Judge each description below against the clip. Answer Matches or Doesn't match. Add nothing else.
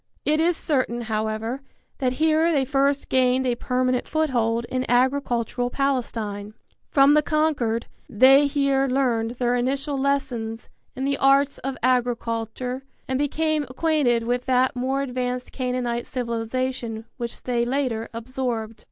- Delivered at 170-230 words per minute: Doesn't match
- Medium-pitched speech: Doesn't match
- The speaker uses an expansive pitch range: Doesn't match